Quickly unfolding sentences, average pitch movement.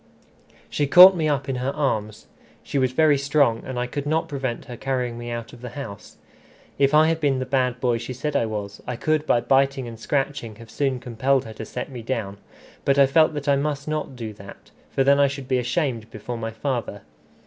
Yes: fast, 225 wpm; average, 3.3 semitones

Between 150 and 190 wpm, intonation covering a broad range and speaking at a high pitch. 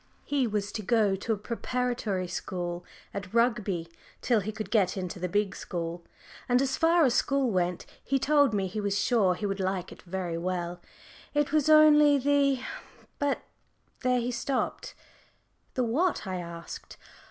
Yes: average, 165 wpm; wide, 6.0 semitones; high, 215 Hz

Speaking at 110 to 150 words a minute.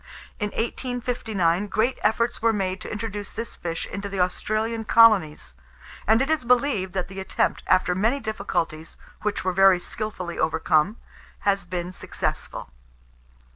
Yes: average, 140 wpm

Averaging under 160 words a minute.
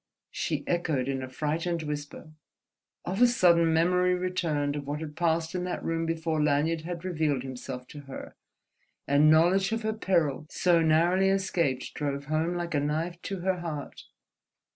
No: average, 165 wpm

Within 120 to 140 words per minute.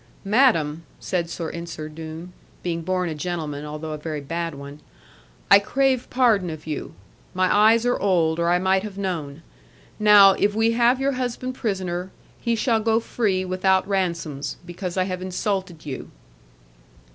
No: average, 160 wpm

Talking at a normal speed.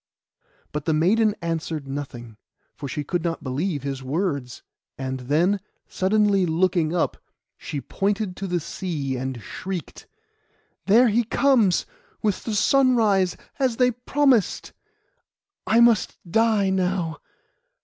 No: slow, 125 wpm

